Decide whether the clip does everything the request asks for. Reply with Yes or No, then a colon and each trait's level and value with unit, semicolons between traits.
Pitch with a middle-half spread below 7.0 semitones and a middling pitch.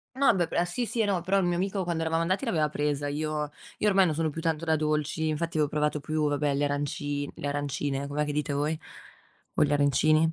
Yes: narrow, 2.6 semitones; medium, 155 Hz